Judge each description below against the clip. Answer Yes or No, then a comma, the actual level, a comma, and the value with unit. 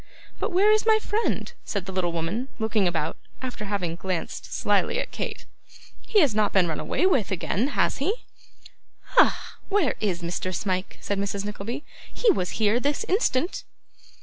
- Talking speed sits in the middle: Yes, average, 170 wpm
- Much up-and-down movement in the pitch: Yes, wide, 7.9 semitones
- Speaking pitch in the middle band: No, high, 210 Hz